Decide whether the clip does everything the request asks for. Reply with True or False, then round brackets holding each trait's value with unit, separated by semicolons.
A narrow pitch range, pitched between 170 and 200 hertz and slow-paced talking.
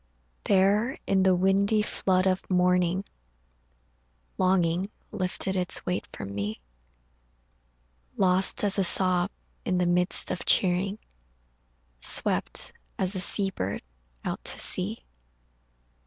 True (1.4 semitones; 185 Hz; 110 wpm)